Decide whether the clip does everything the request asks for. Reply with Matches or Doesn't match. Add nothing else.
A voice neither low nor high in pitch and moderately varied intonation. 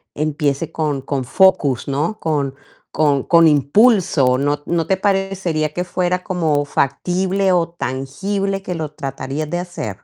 Matches